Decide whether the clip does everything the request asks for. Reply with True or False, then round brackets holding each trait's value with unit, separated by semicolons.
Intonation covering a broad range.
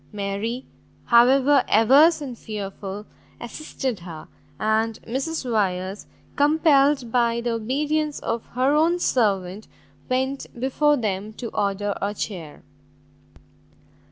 False (5.0 semitones)